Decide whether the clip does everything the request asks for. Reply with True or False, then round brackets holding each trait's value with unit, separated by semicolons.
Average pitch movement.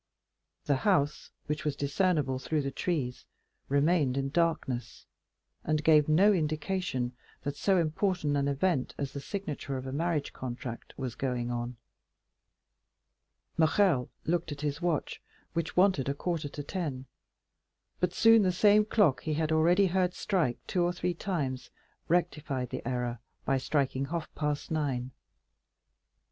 True (4.5 semitones)